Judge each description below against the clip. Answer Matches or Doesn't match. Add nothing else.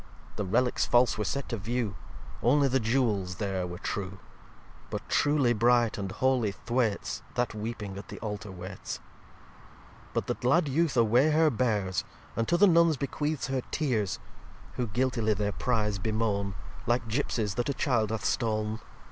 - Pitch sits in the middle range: Doesn't match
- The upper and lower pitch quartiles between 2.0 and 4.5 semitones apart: Matches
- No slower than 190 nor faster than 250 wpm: Doesn't match